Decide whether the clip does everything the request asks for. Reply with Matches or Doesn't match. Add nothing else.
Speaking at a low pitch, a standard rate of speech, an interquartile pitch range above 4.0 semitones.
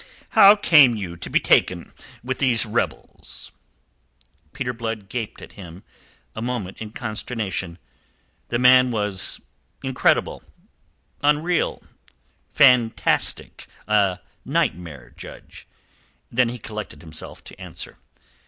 Doesn't match